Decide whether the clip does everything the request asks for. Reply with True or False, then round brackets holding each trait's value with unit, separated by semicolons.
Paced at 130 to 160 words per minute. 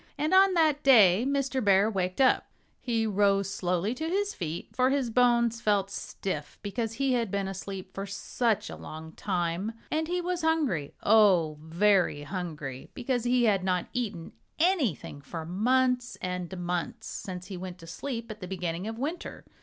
False (170 wpm)